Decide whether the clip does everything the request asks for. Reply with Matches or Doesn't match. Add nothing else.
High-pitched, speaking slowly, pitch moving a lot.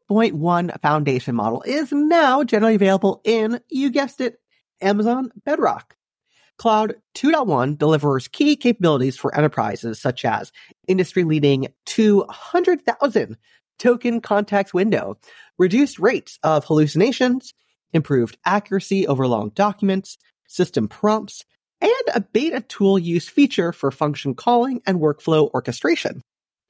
Matches